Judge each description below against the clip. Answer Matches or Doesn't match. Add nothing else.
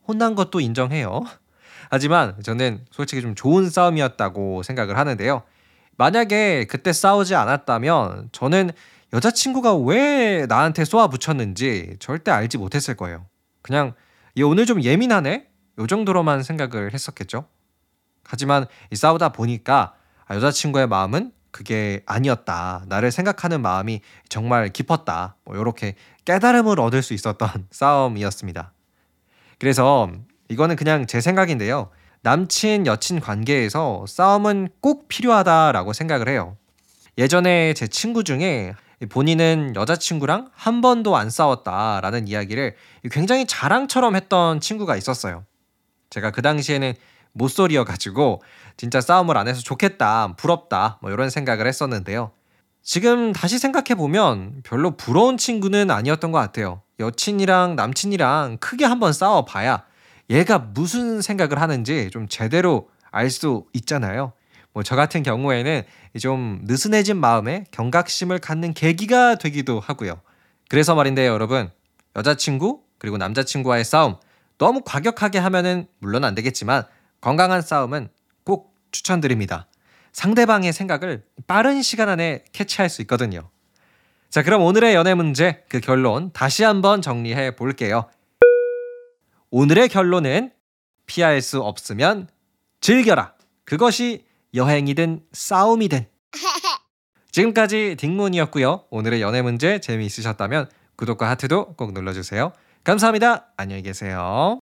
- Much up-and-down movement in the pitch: Matches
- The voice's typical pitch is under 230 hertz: Matches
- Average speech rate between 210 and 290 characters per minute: Doesn't match